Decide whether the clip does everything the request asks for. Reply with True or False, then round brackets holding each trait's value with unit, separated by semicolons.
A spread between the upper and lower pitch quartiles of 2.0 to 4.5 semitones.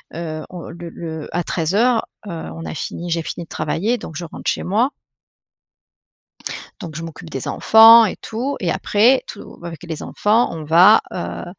False (5.0 semitones)